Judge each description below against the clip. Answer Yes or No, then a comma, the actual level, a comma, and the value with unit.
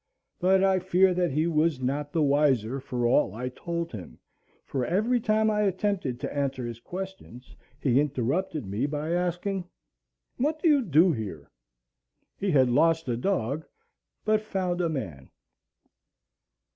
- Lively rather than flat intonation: Yes, wide, 6.6 semitones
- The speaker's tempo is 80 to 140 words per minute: No, average, 150 wpm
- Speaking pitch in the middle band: Yes, medium, 160 Hz